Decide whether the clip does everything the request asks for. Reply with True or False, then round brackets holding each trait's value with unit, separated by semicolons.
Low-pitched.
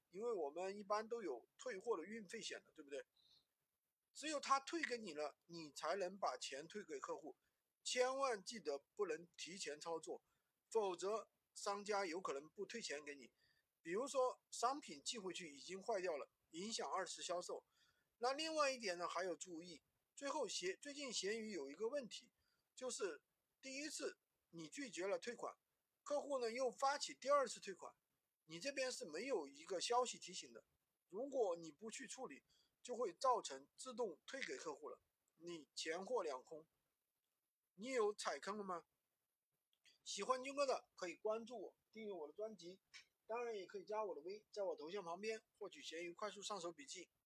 False (230 Hz)